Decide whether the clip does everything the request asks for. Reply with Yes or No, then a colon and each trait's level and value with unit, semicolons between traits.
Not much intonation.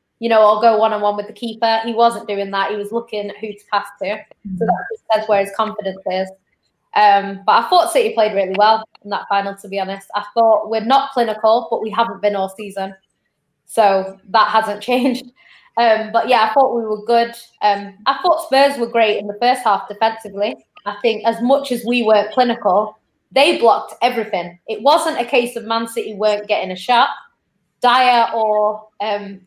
Yes: narrow, 2.3 semitones